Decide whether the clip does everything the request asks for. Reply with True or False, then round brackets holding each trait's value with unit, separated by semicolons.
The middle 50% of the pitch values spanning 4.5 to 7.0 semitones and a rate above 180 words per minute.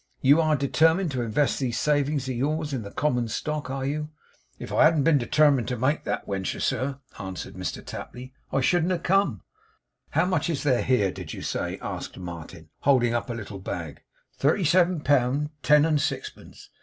False (4.0 semitones; 190 wpm)